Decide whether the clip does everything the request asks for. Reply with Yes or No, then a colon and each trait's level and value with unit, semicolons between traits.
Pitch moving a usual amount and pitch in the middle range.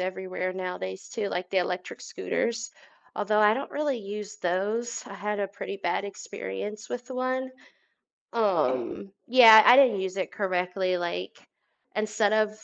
No: average, 3.4 semitones; high, 200 Hz